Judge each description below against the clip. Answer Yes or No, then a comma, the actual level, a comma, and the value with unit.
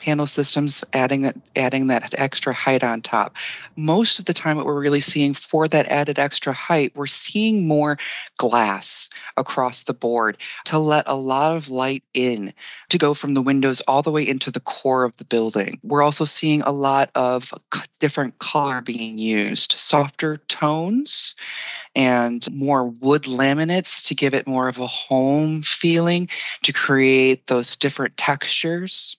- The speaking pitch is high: No, medium, 140 Hz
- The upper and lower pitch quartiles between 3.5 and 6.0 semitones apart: No, average, 2.9 semitones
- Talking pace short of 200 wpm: Yes, average, 165 wpm